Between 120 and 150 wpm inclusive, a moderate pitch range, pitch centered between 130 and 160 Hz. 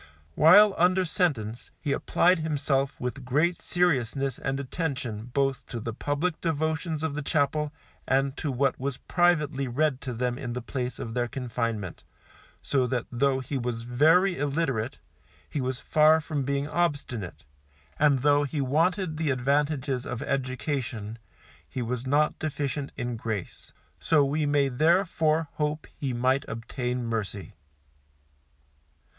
Yes: average, 140 wpm; average, 3.7 semitones; medium, 140 Hz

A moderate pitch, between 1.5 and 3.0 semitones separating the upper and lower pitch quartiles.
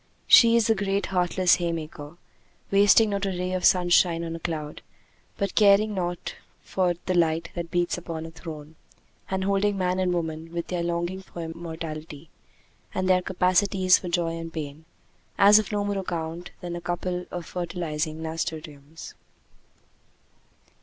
Yes: medium, 175 Hz; narrow, 2.5 semitones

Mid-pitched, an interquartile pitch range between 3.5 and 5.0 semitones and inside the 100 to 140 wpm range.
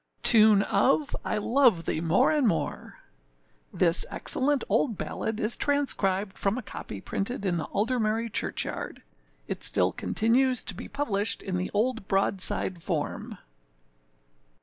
No: high, 215 Hz; average, 4.7 semitones; slow, 135 wpm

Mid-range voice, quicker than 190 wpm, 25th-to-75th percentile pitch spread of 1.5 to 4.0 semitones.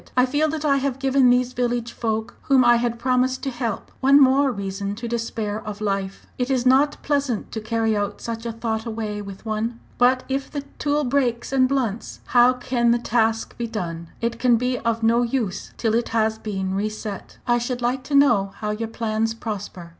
No: high, 235 Hz; fast, 205 wpm; average, 2.7 semitones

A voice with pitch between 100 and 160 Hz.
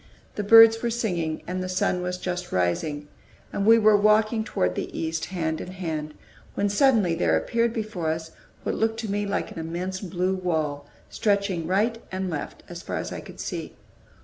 No: medium, 185 Hz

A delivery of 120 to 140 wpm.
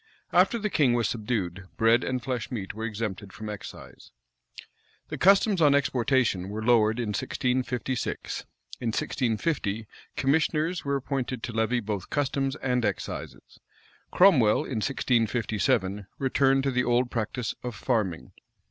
Yes: slow, 135 wpm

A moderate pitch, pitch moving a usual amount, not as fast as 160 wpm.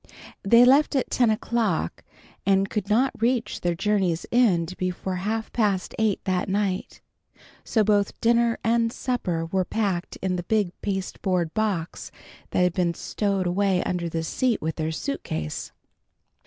No: high, 195 Hz; average, 3.9 semitones; average, 150 wpm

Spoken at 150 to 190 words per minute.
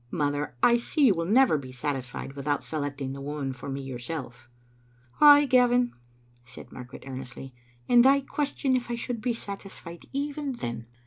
Yes: average, 170 wpm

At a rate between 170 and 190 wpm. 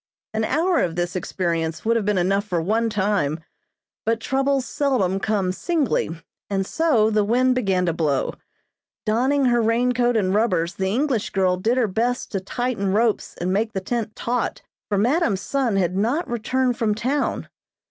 Yes: average, 175 wpm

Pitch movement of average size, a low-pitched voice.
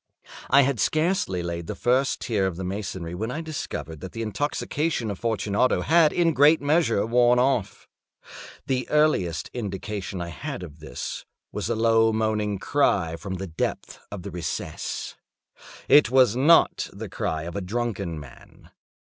No: wide, 6.2 semitones; low, 110 Hz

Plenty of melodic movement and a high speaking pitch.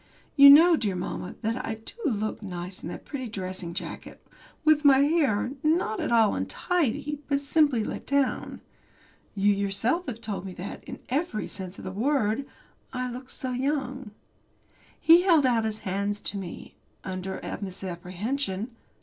Yes: wide, 6.1 semitones; high, 225 Hz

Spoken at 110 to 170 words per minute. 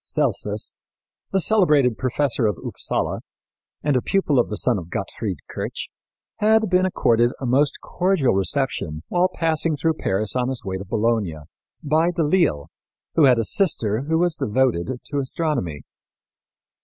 Yes: average, 155 wpm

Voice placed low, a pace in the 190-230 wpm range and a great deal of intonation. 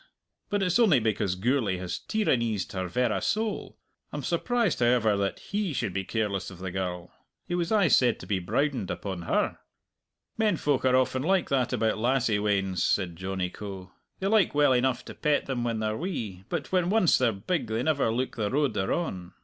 Yes: low, 120 Hz; average, 200 wpm; wide, 7.5 semitones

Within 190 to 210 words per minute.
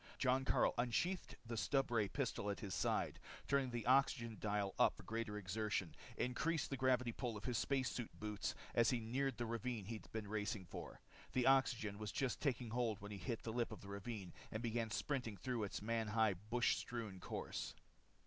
Yes: average, 195 wpm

